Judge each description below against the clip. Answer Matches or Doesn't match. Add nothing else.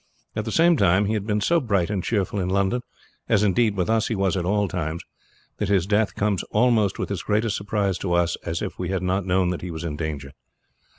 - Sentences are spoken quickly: Matches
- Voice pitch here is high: Doesn't match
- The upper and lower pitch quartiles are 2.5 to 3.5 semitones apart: Matches